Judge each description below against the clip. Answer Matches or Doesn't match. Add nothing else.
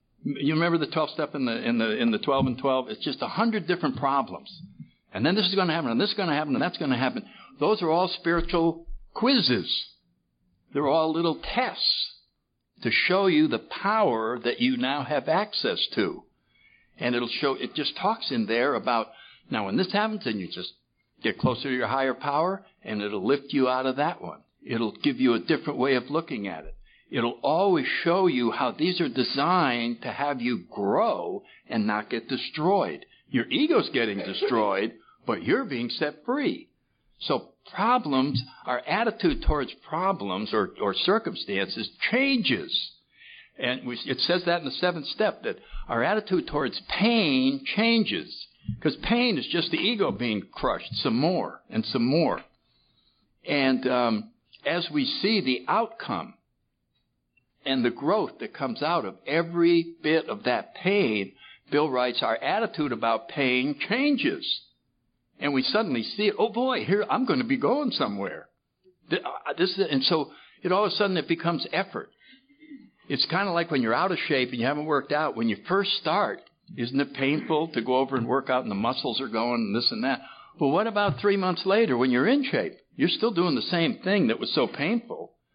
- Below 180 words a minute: Doesn't match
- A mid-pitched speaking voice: Matches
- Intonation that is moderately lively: Doesn't match